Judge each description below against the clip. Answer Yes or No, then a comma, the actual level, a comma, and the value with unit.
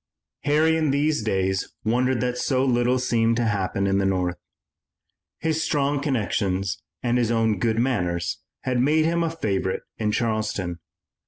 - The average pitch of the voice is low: Yes, low, 115 Hz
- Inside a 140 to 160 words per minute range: Yes, average, 155 wpm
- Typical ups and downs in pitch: No, wide, 5.7 semitones